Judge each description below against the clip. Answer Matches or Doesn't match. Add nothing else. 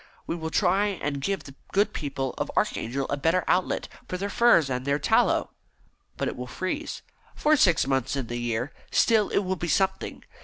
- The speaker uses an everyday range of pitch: Doesn't match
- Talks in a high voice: Doesn't match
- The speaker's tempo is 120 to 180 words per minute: Doesn't match